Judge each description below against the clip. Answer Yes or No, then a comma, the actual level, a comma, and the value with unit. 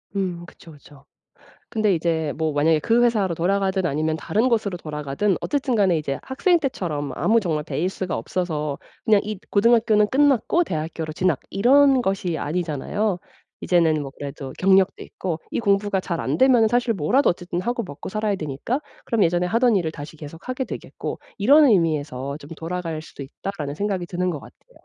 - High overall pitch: No, medium, 180 Hz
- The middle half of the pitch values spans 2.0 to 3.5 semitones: No, wide, 5.6 semitones